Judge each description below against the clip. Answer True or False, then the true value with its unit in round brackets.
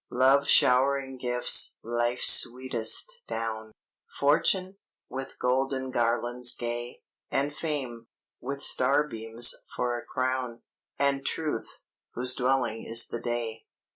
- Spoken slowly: True (105 wpm)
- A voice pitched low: True (125 Hz)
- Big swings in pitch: False (2.4 semitones)